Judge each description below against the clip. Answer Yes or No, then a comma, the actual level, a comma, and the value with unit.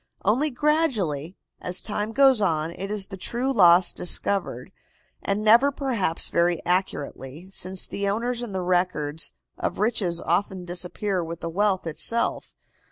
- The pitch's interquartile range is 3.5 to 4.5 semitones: Yes, average, 4.2 semitones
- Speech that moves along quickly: No, average, 140 wpm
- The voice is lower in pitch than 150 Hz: No, high, 190 Hz